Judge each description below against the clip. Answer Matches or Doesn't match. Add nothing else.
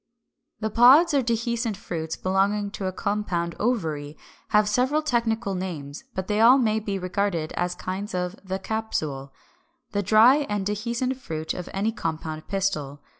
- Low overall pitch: Doesn't match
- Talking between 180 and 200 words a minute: Doesn't match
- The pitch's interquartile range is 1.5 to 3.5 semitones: Doesn't match